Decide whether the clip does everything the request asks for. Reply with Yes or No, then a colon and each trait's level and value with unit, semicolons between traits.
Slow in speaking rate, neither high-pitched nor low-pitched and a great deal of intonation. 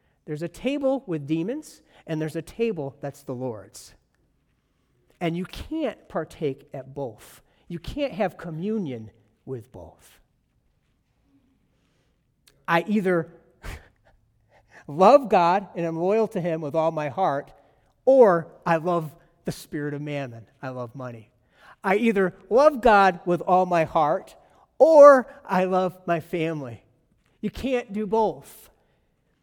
Yes: slow, 130 wpm; medium, 165 Hz; wide, 6.0 semitones